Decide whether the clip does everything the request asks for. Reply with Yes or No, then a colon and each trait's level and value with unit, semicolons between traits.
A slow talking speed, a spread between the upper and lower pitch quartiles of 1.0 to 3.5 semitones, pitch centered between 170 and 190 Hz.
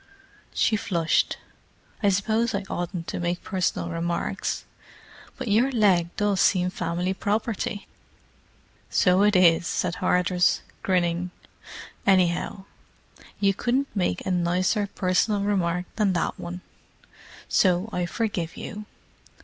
Yes: slow, 115 wpm; average, 2.7 semitones; medium, 185 Hz